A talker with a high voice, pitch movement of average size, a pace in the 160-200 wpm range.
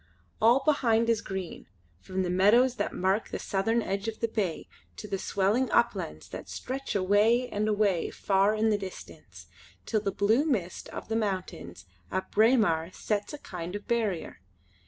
Yes: high, 205 Hz; average, 3.3 semitones; average, 170 wpm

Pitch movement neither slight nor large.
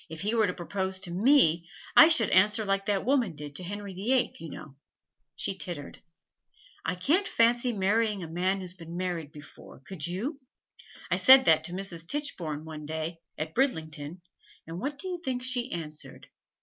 No: wide, 6.1 semitones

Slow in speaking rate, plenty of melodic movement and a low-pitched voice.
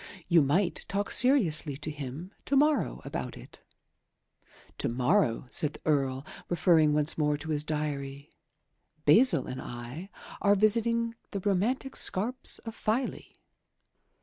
No: slow, 130 wpm; wide, 6.7 semitones; medium, 160 Hz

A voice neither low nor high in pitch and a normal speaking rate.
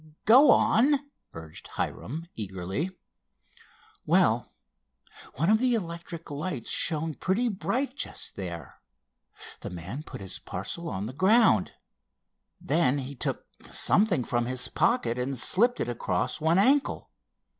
No: medium, 155 Hz; slow, 125 wpm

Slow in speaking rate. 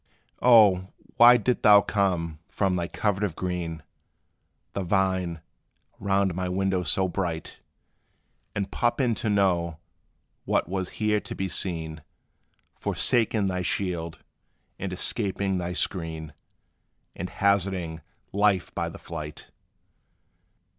Yes: slow, 120 wpm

